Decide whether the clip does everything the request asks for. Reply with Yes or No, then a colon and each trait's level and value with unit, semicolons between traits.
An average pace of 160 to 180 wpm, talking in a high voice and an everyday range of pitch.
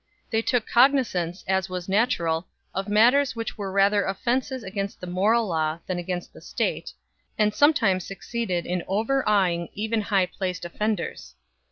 No: average, 150 wpm; high, 200 Hz; average, 3.8 semitones